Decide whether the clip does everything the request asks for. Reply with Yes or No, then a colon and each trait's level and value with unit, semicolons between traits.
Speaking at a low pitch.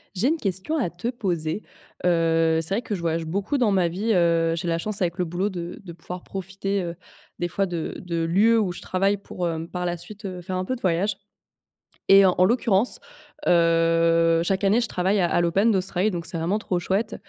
No: medium, 180 Hz